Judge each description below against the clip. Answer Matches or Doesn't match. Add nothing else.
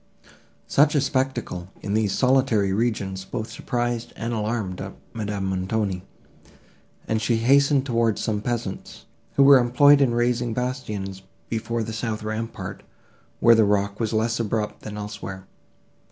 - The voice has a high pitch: Doesn't match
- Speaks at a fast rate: Doesn't match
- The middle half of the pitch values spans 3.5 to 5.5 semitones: Doesn't match